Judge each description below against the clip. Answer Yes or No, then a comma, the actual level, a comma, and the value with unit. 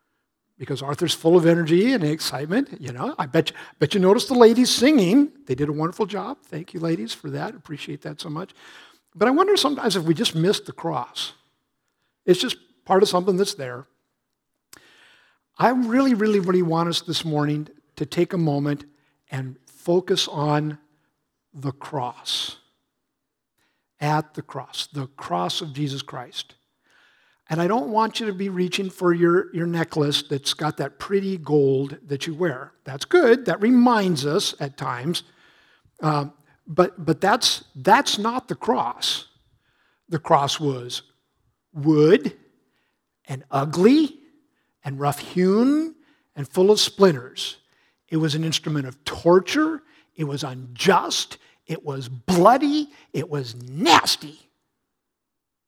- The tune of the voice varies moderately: No, wide, 6.1 semitones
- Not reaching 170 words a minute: Yes, average, 145 wpm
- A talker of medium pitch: Yes, medium, 165 Hz